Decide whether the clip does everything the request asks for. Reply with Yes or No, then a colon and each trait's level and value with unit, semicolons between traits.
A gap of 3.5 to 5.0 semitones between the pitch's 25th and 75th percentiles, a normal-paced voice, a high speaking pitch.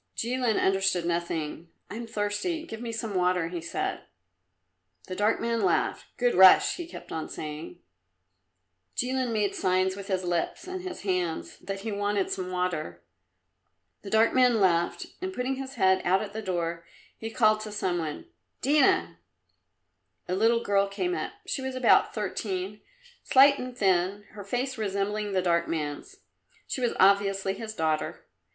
Yes: average, 4.3 semitones; average, 160 wpm; high, 200 Hz